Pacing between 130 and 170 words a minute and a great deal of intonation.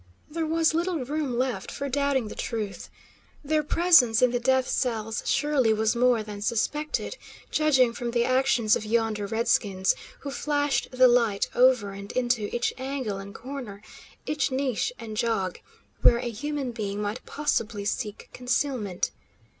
No: average, 155 wpm; average, 4.5 semitones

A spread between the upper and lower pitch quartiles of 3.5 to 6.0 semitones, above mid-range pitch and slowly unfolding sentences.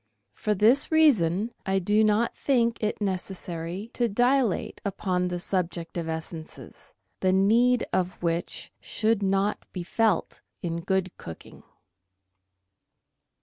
Yes: average, 4.1 semitones; high, 195 Hz; slow, 120 wpm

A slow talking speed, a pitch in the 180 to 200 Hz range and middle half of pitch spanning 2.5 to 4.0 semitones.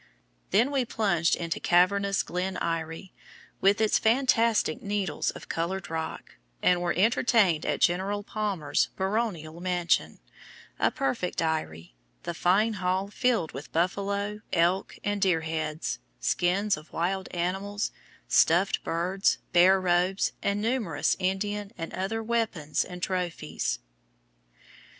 Yes: slow, 120 wpm; medium, 185 Hz; average, 3.3 semitones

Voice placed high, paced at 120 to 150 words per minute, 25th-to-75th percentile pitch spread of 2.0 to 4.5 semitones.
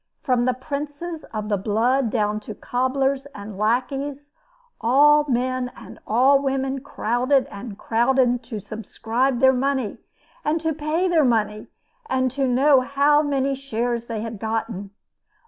Yes: very high, 255 Hz; average, 145 wpm; average, 3.5 semitones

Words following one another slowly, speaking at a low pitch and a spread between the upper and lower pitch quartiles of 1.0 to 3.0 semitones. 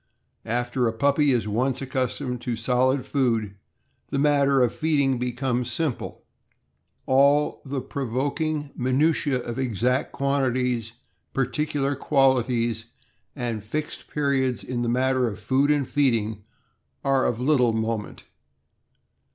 Yes: slow, 120 wpm; low, 130 Hz; narrow, 2.6 semitones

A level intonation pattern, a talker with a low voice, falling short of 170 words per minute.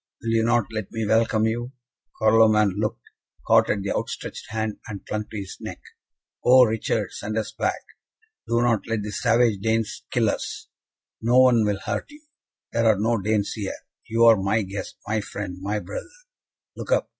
No: narrow, 1.9 semitones; low, 110 Hz; average, 180 wpm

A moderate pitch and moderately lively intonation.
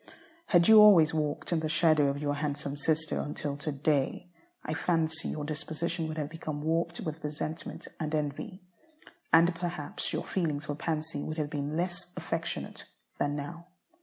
No: medium, 155 Hz; narrow, 2.3 semitones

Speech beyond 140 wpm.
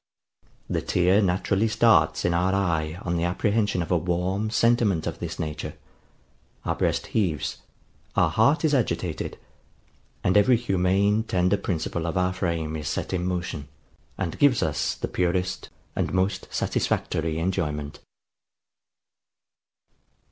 No: slow, 135 wpm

